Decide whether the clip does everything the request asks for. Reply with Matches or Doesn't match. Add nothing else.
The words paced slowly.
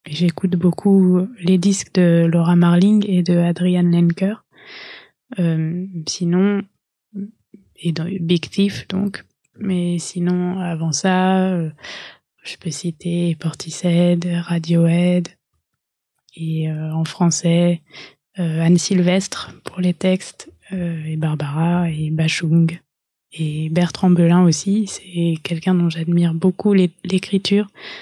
Matches